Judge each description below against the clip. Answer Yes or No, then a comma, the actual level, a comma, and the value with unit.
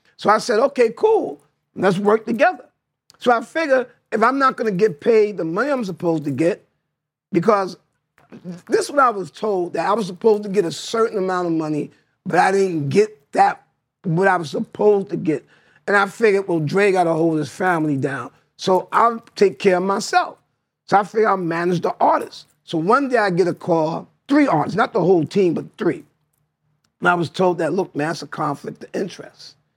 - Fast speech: Yes, fast, 210 wpm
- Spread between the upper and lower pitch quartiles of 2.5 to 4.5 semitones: No, average, 5.2 semitones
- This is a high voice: Yes, high, 195 Hz